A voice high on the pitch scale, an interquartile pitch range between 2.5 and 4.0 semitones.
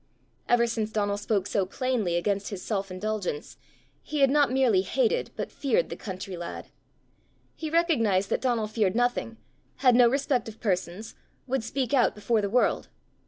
No: high, 225 Hz; average, 4.4 semitones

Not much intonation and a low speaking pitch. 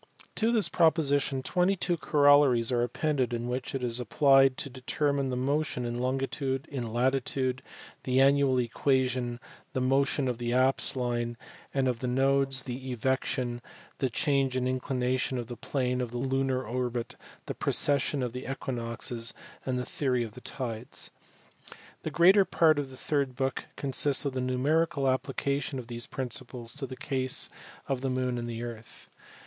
Yes: narrow, 1.9 semitones; low, 130 Hz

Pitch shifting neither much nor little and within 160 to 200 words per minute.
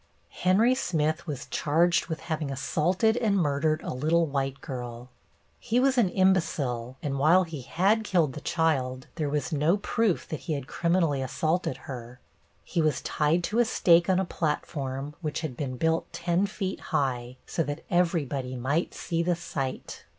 Yes: average, 4.4 semitones; average, 170 wpm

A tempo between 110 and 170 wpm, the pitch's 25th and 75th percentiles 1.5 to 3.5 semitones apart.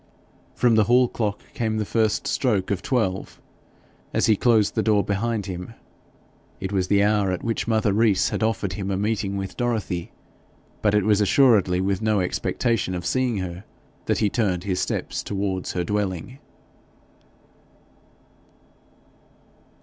Yes: average, 150 wpm; average, 2.9 semitones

